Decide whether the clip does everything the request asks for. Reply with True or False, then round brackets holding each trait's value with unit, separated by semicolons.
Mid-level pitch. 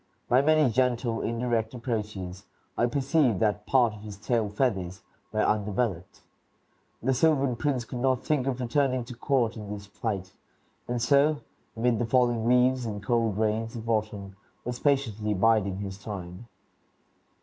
False (115 Hz)